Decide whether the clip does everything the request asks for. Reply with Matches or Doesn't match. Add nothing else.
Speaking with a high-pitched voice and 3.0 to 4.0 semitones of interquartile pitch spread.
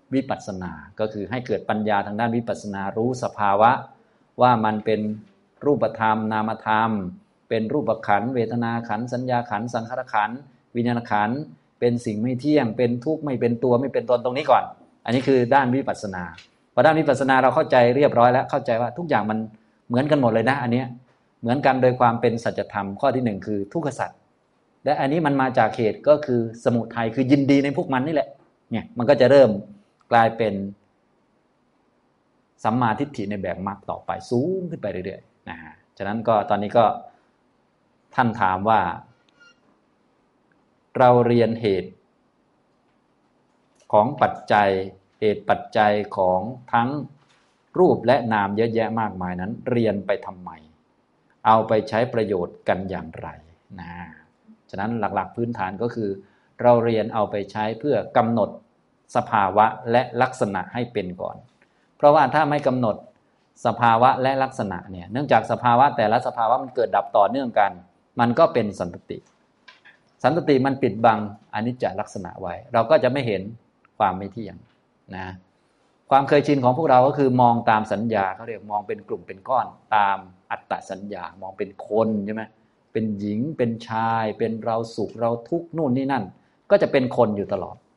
Doesn't match